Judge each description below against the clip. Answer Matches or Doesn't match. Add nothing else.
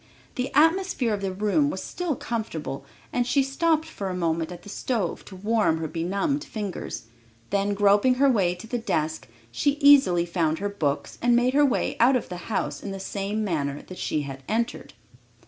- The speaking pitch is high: Matches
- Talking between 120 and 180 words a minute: Doesn't match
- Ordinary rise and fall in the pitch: Doesn't match